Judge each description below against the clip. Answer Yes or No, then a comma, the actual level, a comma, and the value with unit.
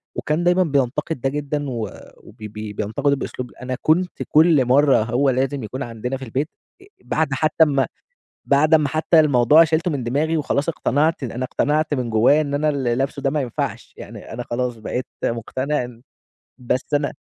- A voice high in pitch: No, medium, 140 Hz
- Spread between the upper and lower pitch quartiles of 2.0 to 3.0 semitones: No, average, 3.5 semitones